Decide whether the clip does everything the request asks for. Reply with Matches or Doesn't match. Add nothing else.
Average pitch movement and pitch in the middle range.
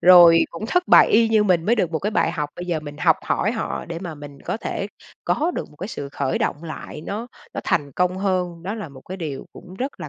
Matches